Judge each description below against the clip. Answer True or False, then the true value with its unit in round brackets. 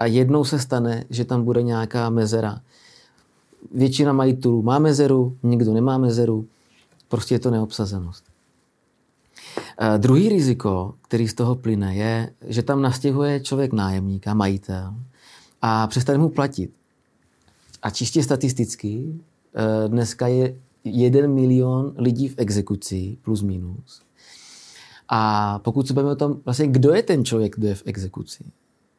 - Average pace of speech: True (135 wpm)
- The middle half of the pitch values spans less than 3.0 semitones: False (3.3 semitones)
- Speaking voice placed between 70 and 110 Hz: False (120 Hz)